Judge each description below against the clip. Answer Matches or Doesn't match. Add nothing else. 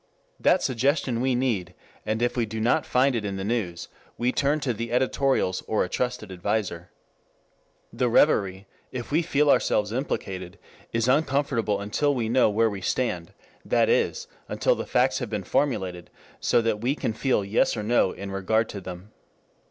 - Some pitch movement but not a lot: Matches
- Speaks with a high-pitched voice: Doesn't match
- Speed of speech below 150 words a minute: Doesn't match